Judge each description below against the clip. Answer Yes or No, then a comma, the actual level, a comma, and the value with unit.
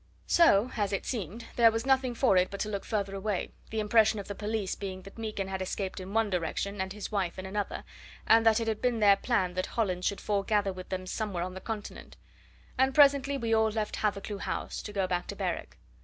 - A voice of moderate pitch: No, high, 205 Hz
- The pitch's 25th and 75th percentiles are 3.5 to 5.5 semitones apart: No, average, 2.8 semitones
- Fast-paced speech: Yes, fast, 230 wpm